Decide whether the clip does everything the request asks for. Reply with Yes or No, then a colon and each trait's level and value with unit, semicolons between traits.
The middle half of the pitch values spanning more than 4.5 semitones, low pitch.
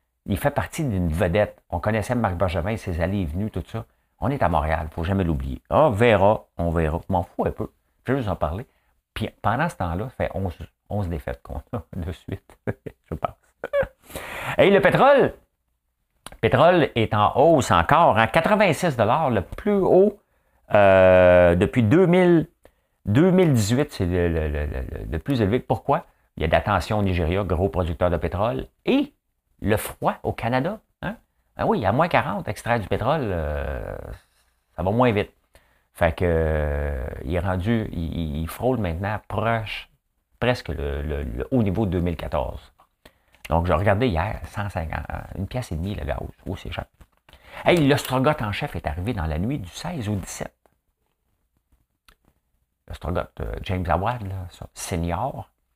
Yes: wide, 5.5 semitones; very low, 95 Hz